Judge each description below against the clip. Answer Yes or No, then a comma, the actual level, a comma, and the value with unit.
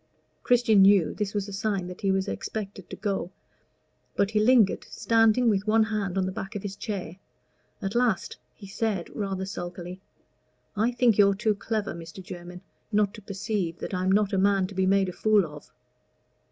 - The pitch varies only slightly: Yes, narrow, 2.2 semitones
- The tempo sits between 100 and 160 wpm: No, average, 190 wpm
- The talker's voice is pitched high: Yes, high, 200 Hz